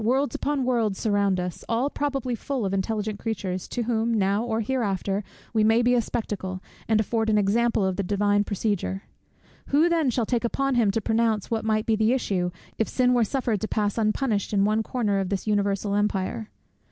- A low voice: No, high, 220 Hz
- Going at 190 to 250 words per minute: Yes, average, 200 wpm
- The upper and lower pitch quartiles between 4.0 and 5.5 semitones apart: No, average, 2.8 semitones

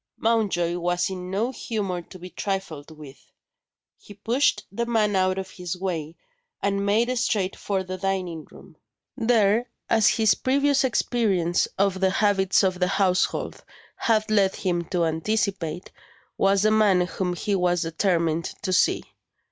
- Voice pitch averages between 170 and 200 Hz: Yes, high, 190 Hz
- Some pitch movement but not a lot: Yes, average, 3.2 semitones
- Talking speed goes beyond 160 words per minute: No, average, 150 wpm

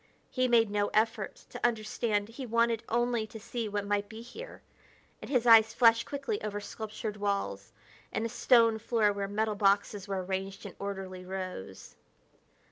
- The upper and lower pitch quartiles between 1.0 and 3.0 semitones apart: Yes, narrow, 2.5 semitones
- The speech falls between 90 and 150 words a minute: No, average, 165 wpm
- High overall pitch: Yes, high, 215 Hz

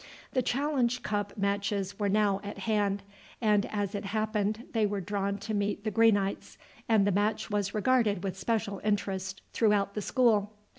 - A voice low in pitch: No, high, 205 Hz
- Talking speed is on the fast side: No, average, 165 wpm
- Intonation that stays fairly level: Yes, narrow, 1.5 semitones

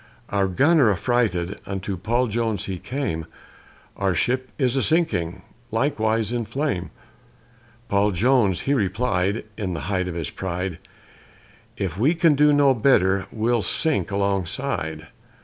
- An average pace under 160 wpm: Yes, average, 140 wpm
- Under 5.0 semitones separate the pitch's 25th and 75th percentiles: No, wide, 5.6 semitones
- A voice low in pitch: Yes, low, 105 Hz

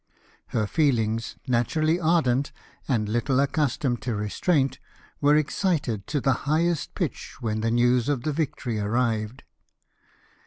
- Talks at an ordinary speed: No, slow, 125 wpm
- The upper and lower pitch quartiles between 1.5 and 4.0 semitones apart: No, average, 4.7 semitones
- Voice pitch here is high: No, low, 130 Hz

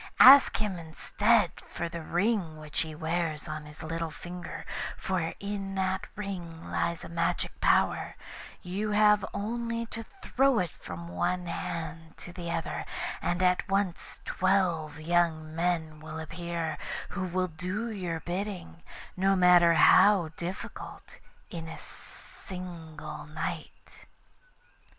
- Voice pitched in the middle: Yes, medium, 175 Hz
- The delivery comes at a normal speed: No, slow, 130 wpm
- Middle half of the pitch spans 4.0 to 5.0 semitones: No, average, 3.2 semitones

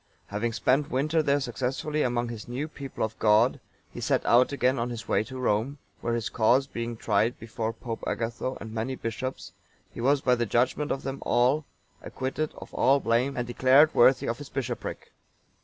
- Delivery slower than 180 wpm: No, average, 195 wpm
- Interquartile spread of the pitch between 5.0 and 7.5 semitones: No, average, 2.8 semitones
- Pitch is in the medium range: No, low, 125 Hz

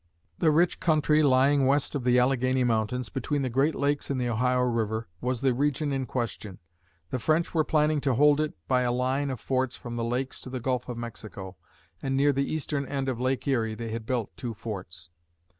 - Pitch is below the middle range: Yes, low, 130 Hz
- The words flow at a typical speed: No, fast, 210 wpm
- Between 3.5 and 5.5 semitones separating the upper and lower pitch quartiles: No, average, 3.1 semitones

